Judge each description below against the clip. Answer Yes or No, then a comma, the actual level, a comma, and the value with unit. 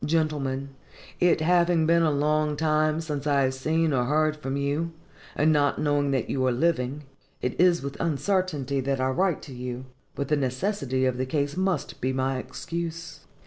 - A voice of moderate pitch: Yes, medium, 145 Hz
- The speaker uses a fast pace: No, average, 185 wpm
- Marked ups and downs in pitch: No, average, 3.4 semitones